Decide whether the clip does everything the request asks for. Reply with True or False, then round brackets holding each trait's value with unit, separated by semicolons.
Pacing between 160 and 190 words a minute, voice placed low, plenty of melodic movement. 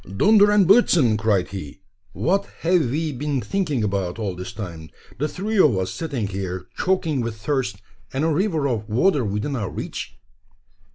True (170 wpm; 125 Hz; 8.6 semitones)